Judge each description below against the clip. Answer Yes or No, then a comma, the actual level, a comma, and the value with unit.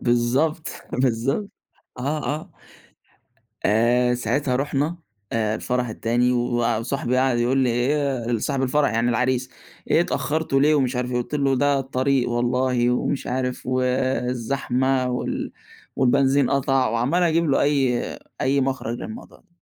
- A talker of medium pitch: No, low, 130 Hz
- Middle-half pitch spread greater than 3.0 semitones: No, narrow, 2.4 semitones